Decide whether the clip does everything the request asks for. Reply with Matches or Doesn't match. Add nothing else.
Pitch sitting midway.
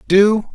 Doesn't match